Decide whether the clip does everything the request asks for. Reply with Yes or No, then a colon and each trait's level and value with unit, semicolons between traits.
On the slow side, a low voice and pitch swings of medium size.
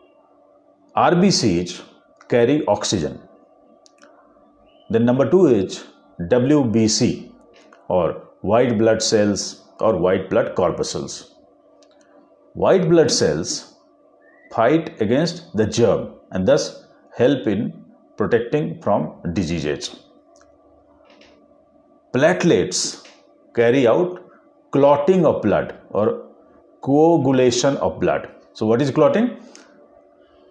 No: slow, 85 wpm; low, 125 Hz; wide, 6.2 semitones